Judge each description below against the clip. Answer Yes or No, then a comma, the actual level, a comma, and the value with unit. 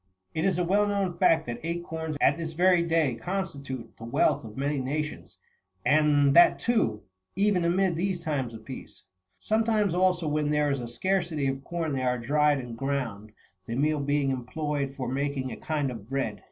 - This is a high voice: No, medium, 150 Hz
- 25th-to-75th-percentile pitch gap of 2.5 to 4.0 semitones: No, average, 4.4 semitones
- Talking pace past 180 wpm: Yes, average, 190 wpm